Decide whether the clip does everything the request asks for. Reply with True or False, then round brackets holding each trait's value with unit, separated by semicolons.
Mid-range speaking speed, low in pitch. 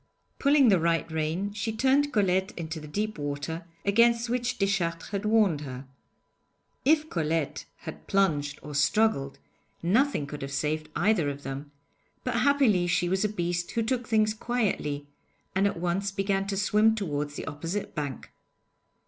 False (155 wpm; 190 Hz)